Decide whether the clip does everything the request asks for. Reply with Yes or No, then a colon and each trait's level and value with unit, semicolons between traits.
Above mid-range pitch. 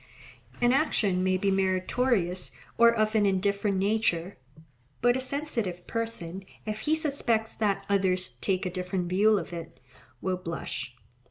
Yes: high, 195 Hz